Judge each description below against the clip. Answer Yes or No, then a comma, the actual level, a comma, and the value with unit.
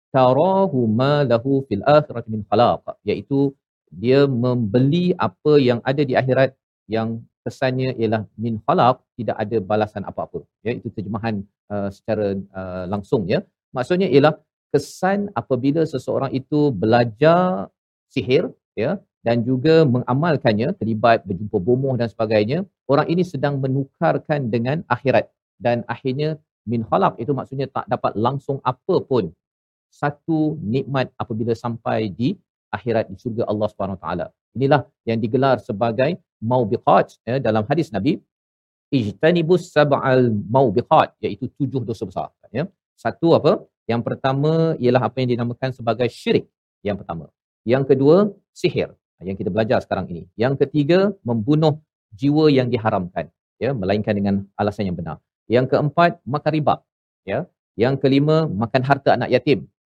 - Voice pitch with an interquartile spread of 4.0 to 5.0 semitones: Yes, average, 4.3 semitones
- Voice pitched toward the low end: Yes, low, 130 Hz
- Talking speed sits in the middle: No, fast, 135 wpm